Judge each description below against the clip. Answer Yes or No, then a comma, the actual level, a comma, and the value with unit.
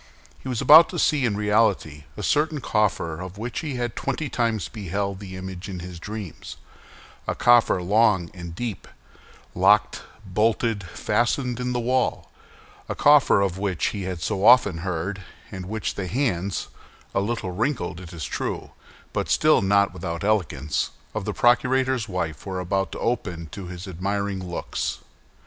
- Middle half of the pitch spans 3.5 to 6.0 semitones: Yes, average, 4.4 semitones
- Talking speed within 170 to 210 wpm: No, average, 155 wpm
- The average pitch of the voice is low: Yes, low, 100 Hz